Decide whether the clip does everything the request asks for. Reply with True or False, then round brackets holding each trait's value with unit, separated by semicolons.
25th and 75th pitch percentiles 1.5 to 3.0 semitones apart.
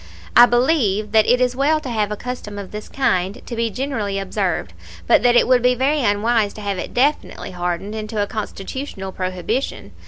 False (3.9 semitones)